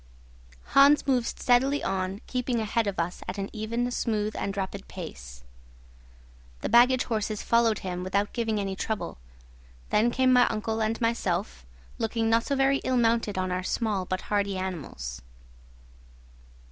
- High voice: Yes, high, 215 Hz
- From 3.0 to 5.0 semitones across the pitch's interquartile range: Yes, average, 3.8 semitones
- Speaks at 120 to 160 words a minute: Yes, average, 150 wpm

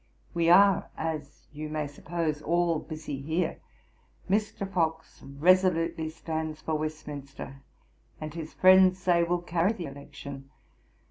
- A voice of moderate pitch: Yes, medium, 160 Hz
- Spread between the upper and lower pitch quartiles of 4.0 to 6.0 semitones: No, narrow, 2.6 semitones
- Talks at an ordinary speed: No, slow, 125 wpm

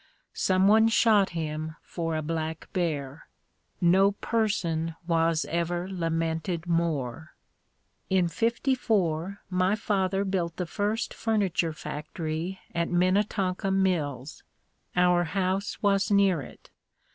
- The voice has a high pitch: No, medium, 180 Hz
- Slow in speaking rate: Yes, slow, 105 wpm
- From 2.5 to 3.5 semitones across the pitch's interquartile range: Yes, average, 3.2 semitones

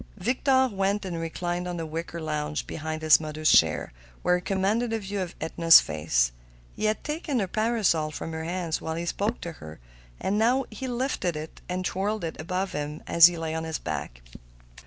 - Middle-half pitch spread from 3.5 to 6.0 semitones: Yes, average, 4.6 semitones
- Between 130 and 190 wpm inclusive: No, average, 200 wpm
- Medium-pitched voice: Yes, medium, 175 Hz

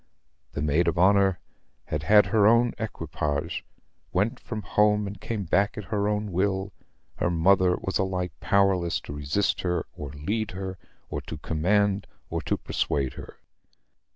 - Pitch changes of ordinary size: Yes, average, 3.3 semitones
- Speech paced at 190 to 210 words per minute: No, average, 155 wpm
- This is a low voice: Yes, very low, 95 Hz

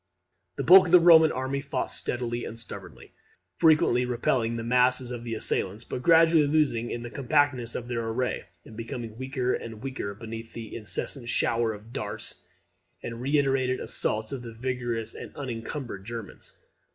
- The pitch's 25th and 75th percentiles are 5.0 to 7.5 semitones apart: No, average, 2.9 semitones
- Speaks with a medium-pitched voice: No, low, 120 Hz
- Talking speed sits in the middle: Yes, average, 165 wpm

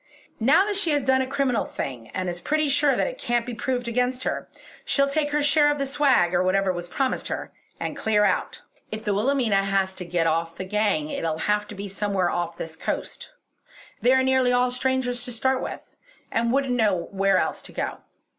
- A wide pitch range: Yes, wide, 5.7 semitones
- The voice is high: Yes, high, 235 Hz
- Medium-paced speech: No, fast, 215 wpm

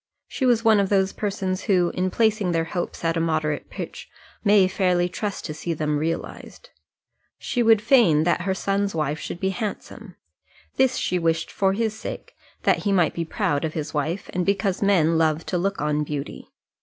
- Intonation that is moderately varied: Yes, average, 3.7 semitones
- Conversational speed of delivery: Yes, average, 195 wpm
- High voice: No, medium, 180 Hz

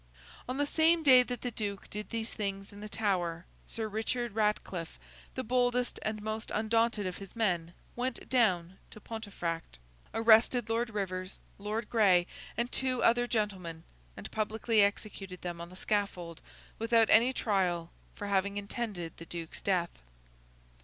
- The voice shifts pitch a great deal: No, average, 3.8 semitones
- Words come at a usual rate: Yes, average, 155 wpm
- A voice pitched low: No, high, 210 Hz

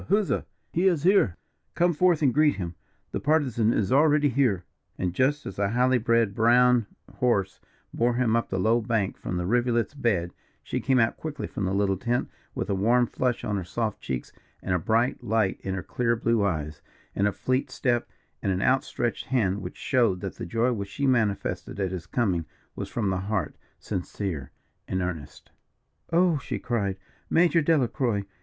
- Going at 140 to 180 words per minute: No, average, 190 wpm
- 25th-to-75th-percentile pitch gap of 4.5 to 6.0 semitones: Yes, average, 4.8 semitones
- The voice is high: No, low, 115 Hz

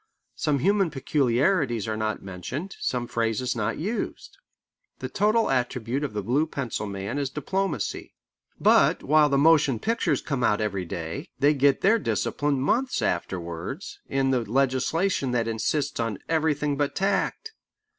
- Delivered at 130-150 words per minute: Yes, average, 145 wpm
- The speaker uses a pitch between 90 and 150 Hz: Yes, low, 135 Hz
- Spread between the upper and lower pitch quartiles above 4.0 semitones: Yes, wide, 5.4 semitones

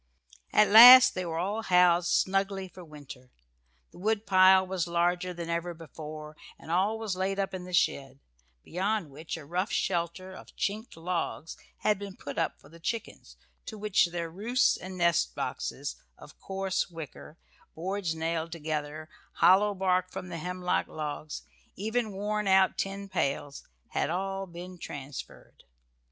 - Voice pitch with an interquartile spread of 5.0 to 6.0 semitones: No, average, 3.0 semitones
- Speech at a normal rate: Yes, average, 150 wpm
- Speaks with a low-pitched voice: No, medium, 180 Hz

